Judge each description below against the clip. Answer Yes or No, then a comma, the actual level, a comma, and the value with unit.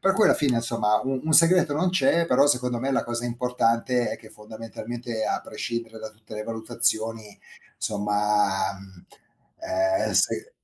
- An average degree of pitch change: Yes, average, 3.0 semitones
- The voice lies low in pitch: Yes, low, 115 Hz